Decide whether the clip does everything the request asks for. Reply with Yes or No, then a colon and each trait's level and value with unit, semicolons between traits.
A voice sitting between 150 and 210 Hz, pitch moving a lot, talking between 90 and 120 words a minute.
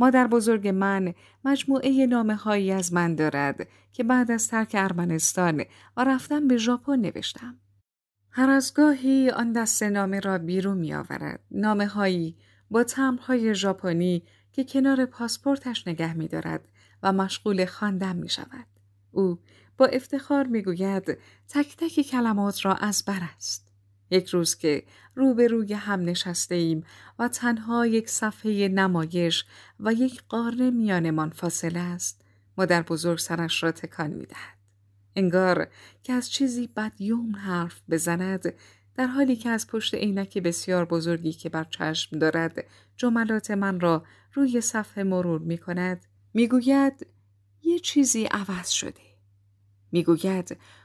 No: high, 190 Hz; wide, 6.2 semitones; average, 140 wpm